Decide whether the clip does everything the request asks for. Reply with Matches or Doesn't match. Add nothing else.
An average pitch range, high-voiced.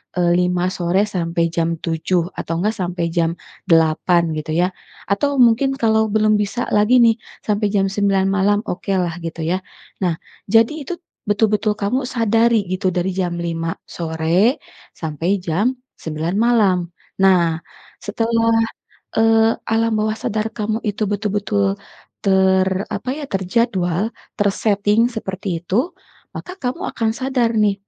Matches